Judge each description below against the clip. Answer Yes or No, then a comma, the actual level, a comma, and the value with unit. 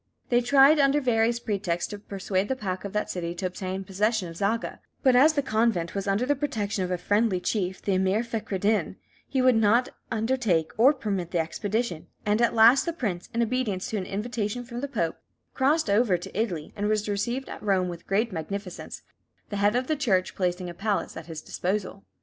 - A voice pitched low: No, high, 210 Hz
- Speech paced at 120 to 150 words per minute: No, fast, 205 wpm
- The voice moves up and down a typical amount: Yes, average, 4.3 semitones